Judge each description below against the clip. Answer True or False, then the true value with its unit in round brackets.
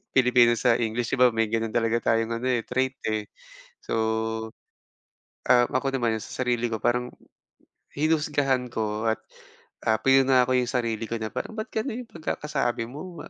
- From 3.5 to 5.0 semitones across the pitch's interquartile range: False (2.9 semitones)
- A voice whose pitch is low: True (125 Hz)